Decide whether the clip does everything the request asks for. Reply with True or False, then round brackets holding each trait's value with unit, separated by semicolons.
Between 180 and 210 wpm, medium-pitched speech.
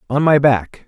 False (205 wpm; 130 Hz)